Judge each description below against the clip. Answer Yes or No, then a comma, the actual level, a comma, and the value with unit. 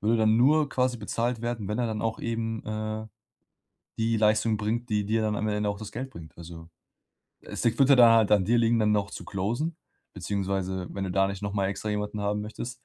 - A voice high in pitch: No, low, 110 Hz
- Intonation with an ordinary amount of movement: No, narrow, 2.2 semitones